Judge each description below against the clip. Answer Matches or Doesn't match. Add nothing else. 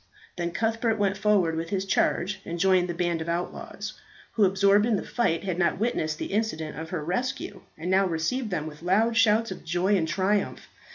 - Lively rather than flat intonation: Doesn't match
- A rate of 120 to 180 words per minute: Doesn't match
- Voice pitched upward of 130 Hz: Matches